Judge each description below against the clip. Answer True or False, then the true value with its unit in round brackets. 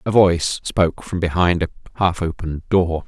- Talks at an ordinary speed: True (175 wpm)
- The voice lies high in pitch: False (85 Hz)